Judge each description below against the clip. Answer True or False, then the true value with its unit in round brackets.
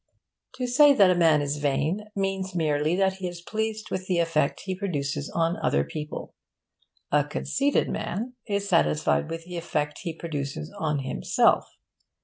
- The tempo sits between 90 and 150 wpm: False (160 wpm)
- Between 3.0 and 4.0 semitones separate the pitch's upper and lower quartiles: False (4.7 semitones)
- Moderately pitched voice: True (170 Hz)